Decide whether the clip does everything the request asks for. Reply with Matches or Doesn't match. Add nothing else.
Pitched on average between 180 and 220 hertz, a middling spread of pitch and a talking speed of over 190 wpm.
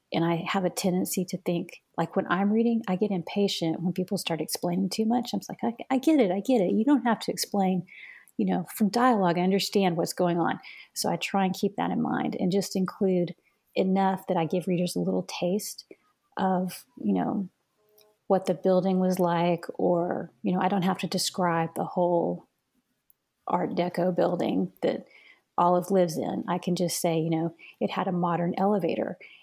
Doesn't match